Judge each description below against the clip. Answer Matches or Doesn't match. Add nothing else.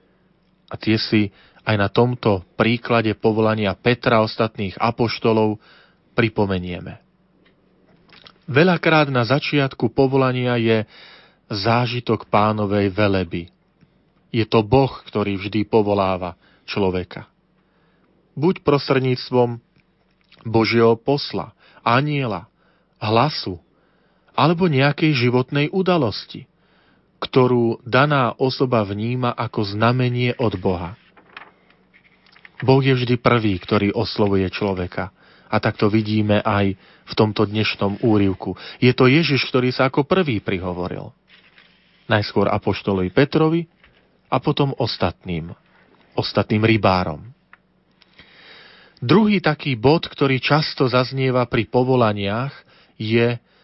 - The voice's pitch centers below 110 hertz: Doesn't match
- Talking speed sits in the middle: Doesn't match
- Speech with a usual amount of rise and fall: Matches